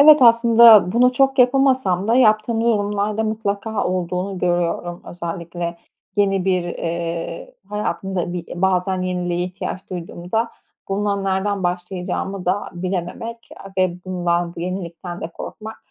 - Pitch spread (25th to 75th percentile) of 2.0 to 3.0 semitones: No, average, 3.6 semitones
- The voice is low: No, high, 190 Hz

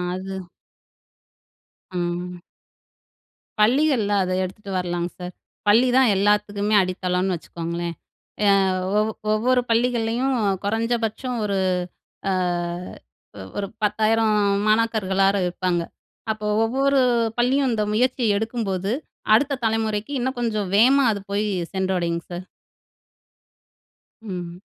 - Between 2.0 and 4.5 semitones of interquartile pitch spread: Yes, average, 3.8 semitones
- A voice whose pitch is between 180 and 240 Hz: Yes, high, 210 Hz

